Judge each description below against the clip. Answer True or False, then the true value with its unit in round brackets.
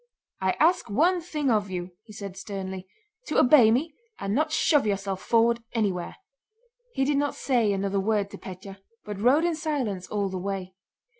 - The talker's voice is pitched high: True (210 Hz)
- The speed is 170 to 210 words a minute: True (175 wpm)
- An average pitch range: False (6.4 semitones)